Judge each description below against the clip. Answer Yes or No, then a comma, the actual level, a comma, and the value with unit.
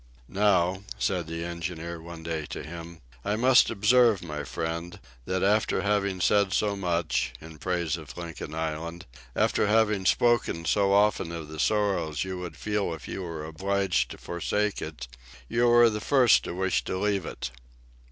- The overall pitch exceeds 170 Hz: No, very low, 90 Hz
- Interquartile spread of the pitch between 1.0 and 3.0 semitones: No, average, 3.8 semitones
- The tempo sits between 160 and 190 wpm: Yes, average, 170 wpm